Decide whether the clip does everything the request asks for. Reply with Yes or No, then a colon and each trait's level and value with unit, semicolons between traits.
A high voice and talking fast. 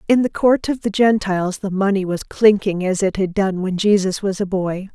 Yes: high, 195 Hz; fast, 230 wpm